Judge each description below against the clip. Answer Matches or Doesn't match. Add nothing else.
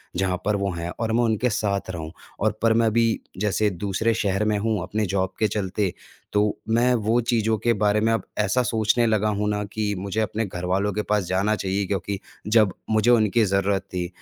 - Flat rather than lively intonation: Matches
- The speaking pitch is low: Matches